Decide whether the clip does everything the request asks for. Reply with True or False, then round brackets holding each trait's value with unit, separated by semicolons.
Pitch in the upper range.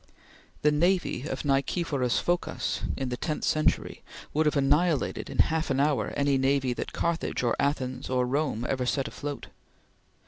False (140 Hz)